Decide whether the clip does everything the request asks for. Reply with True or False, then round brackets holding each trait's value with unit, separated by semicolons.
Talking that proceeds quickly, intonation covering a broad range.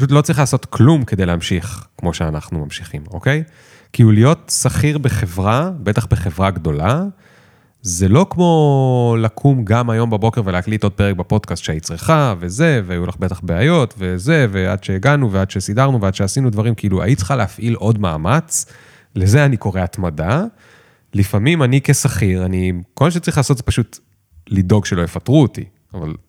True (160 wpm; 6.3 semitones)